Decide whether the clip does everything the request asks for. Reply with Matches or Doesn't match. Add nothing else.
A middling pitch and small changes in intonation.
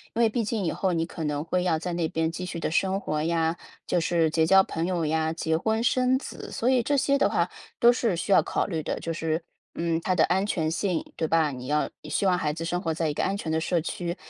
Doesn't match